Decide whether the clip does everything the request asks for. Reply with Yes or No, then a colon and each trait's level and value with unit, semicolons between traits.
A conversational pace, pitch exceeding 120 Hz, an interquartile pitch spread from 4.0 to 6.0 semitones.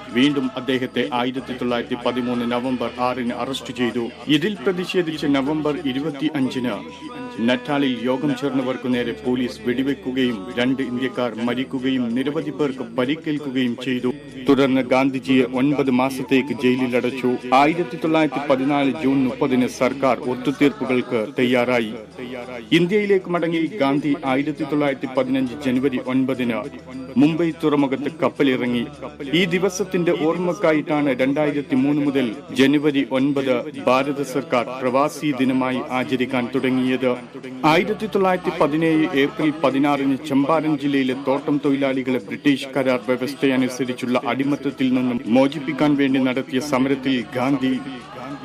No: average, 105 wpm; low, 135 Hz; average, 2.7 semitones